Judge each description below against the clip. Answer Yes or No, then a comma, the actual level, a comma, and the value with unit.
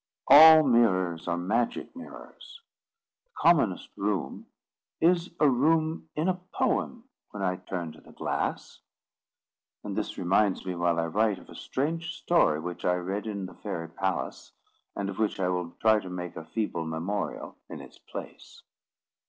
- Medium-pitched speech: No, low, 100 Hz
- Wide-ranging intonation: Yes, wide, 8.2 semitones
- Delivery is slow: No, average, 160 wpm